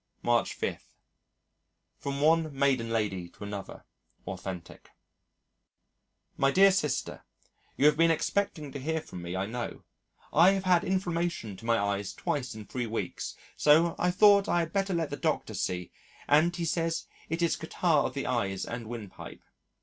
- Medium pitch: Yes, medium, 145 Hz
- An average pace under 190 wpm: Yes, average, 165 wpm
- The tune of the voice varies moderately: No, wide, 7.5 semitones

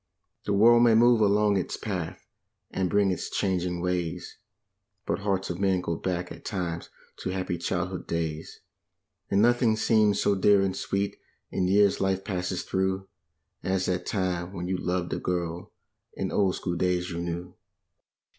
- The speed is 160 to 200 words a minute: Yes, average, 165 wpm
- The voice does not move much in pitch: Yes, narrow, 2.2 semitones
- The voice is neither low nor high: No, very low, 95 Hz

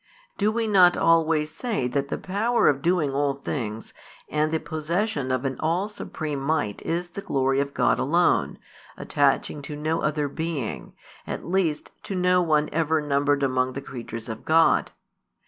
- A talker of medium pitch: Yes, medium, 150 Hz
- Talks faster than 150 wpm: Yes, average, 170 wpm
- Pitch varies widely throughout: No, average, 3.7 semitones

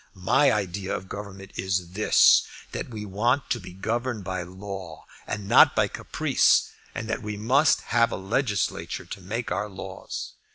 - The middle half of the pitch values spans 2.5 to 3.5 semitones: Yes, average, 3.2 semitones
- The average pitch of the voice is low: Yes, low, 100 Hz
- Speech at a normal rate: Yes, average, 165 wpm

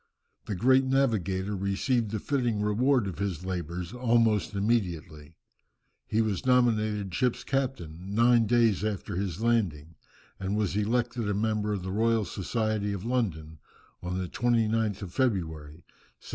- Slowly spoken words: No, average, 145 wpm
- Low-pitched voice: Yes, low, 105 Hz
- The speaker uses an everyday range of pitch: Yes, average, 4.0 semitones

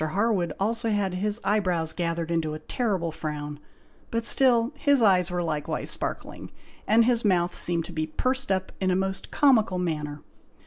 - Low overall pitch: No, medium, 185 Hz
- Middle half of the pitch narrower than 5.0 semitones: No, average, 5.3 semitones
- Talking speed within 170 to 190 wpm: Yes, average, 175 wpm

